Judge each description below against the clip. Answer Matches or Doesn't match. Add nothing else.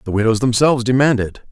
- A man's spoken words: Matches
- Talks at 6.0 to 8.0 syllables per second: Matches